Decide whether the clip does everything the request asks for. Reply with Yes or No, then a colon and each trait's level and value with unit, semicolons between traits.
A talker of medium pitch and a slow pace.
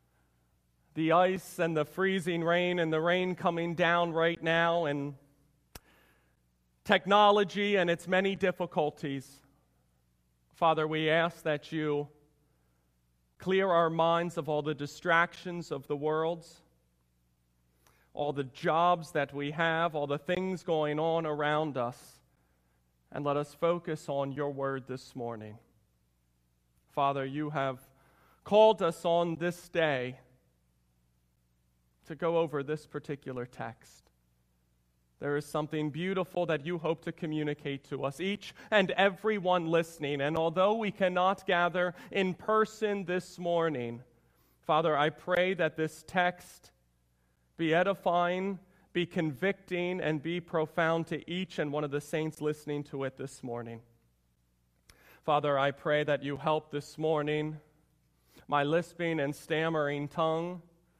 Yes: medium, 155 Hz; slow, 130 wpm